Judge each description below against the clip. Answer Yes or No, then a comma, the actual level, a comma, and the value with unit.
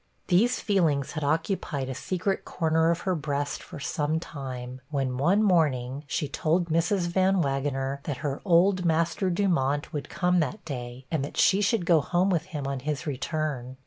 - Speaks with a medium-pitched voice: Yes, medium, 155 Hz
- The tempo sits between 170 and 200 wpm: Yes, average, 175 wpm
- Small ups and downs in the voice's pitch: No, average, 4.4 semitones